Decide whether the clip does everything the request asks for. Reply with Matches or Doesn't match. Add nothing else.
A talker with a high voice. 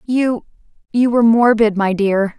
Matches